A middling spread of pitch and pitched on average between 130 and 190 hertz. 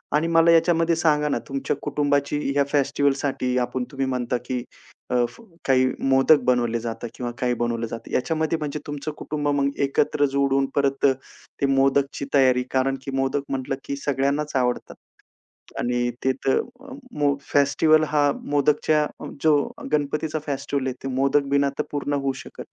No: narrow, 2.0 semitones; medium, 140 Hz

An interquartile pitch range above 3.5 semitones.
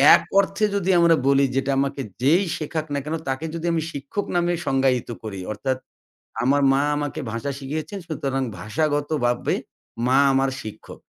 No: average, 3.1 semitones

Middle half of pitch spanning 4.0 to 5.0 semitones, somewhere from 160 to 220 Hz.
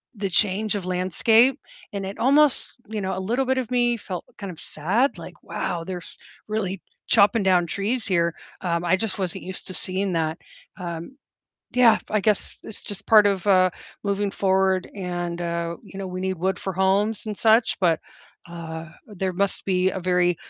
No: average, 2.9 semitones; high, 190 Hz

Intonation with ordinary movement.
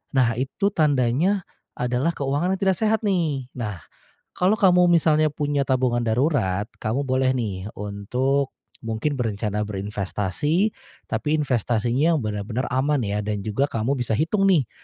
No: wide, 5.9 semitones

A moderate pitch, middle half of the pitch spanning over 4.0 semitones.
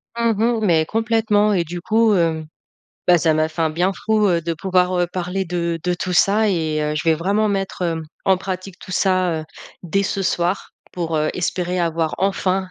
No: medium, 180 Hz; average, 2.7 semitones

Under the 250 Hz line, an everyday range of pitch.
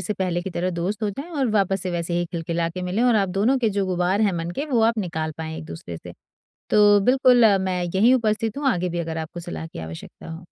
Yes: medium, 185 Hz; average, 4.2 semitones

